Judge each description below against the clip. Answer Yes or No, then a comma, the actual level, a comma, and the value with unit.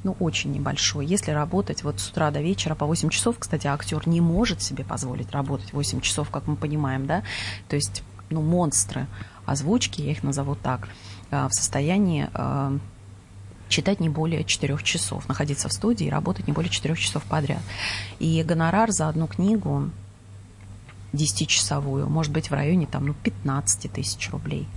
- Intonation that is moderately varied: No, wide, 7.2 semitones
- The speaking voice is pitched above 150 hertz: No, medium, 140 Hz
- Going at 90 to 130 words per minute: No, fast, 160 wpm